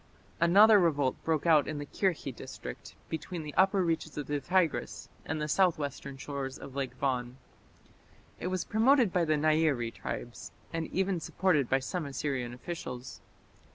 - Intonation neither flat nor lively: Yes, average, 4.5 semitones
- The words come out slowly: No, average, 155 wpm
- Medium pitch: Yes, medium, 155 Hz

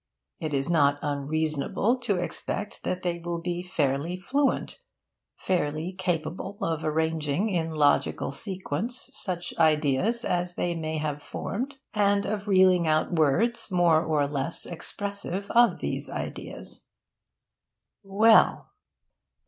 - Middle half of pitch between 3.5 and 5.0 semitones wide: Yes, average, 4.3 semitones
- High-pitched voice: No, medium, 175 Hz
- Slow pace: Yes, slow, 120 wpm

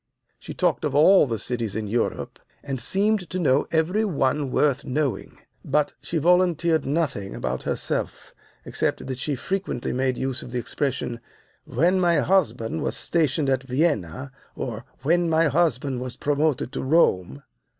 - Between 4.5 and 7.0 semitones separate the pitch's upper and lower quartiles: Yes, average, 5.0 semitones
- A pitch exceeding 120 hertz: Yes, medium, 140 Hz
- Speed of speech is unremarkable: Yes, average, 155 wpm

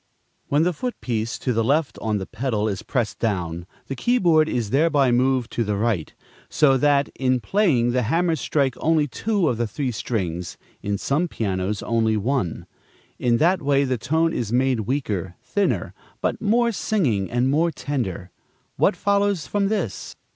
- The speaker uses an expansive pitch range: Yes, wide, 6.4 semitones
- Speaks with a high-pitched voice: No, low, 130 Hz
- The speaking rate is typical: Yes, average, 175 wpm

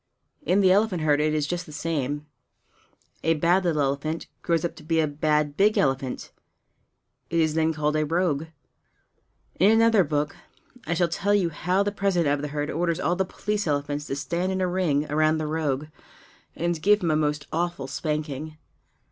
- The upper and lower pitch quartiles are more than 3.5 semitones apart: No, average, 3.0 semitones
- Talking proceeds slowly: No, average, 190 wpm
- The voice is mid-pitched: Yes, medium, 160 Hz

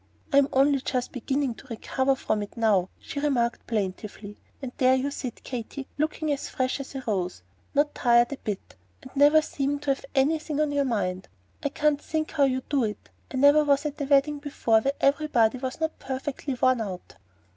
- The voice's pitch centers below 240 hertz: No, very high, 270 Hz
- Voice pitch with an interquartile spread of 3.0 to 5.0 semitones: Yes, average, 3.3 semitones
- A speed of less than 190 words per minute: No, average, 200 wpm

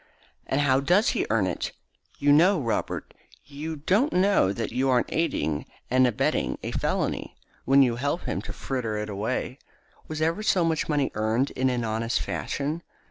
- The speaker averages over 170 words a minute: Yes, average, 180 wpm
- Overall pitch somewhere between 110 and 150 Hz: Yes, low, 135 Hz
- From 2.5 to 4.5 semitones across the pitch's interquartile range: No, wide, 5.5 semitones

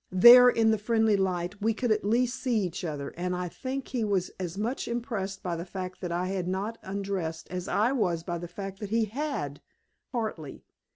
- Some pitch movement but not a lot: Yes, average, 4.1 semitones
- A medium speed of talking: No, fast, 210 wpm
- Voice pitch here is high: Yes, high, 195 Hz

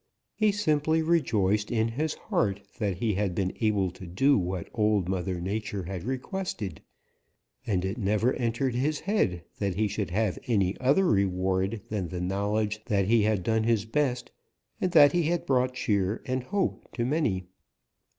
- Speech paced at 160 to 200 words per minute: Yes, average, 170 wpm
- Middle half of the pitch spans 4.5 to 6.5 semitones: Yes, average, 5.2 semitones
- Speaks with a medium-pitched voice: No, low, 110 Hz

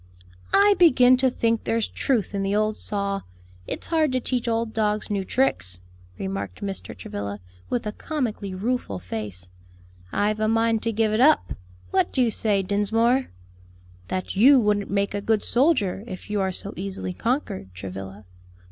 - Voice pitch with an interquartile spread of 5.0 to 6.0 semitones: No, average, 3.8 semitones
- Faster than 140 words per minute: Yes, average, 165 wpm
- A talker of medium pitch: No, high, 210 Hz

